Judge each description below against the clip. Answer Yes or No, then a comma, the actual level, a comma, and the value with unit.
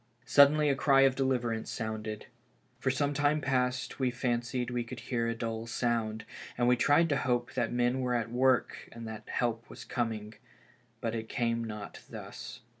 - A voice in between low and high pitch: No, low, 120 Hz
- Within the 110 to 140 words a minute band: No, average, 185 wpm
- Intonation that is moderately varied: No, narrow, 2.3 semitones